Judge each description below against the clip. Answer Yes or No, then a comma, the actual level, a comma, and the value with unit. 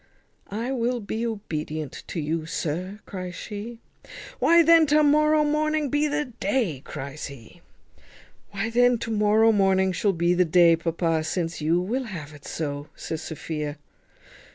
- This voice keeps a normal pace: Yes, average, 155 wpm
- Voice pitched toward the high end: Yes, high, 195 Hz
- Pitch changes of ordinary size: No, wide, 7.0 semitones